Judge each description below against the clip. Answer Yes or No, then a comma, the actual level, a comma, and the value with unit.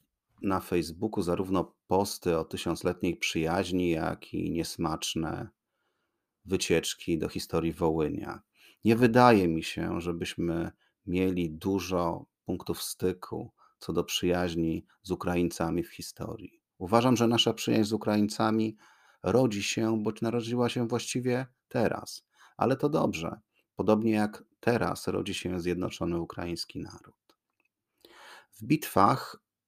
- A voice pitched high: No, very low, 95 Hz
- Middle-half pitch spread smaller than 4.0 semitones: No, average, 4.3 semitones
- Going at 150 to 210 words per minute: No, average, 115 wpm